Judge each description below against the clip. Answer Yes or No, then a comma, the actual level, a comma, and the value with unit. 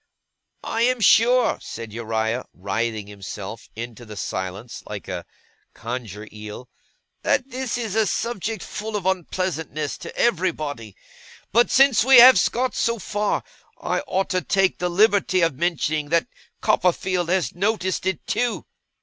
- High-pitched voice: No, medium, 180 Hz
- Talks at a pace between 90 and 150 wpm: Yes, average, 140 wpm